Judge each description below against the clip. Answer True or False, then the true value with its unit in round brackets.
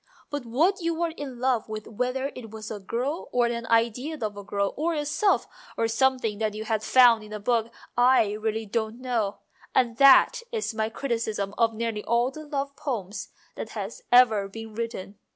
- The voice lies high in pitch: True (230 Hz)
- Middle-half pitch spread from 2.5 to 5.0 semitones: True (3.4 semitones)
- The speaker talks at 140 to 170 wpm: False (195 wpm)